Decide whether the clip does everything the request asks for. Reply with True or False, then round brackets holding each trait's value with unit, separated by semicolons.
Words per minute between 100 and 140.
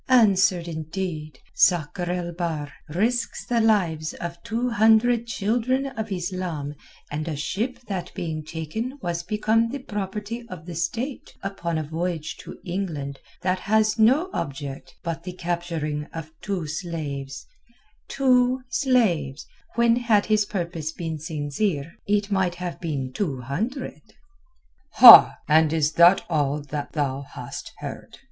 True (135 wpm)